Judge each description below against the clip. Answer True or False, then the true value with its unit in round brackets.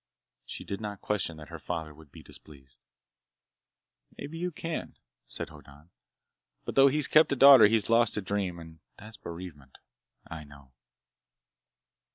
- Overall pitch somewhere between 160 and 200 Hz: False (95 Hz)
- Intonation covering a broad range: True (7.0 semitones)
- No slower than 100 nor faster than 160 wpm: True (150 wpm)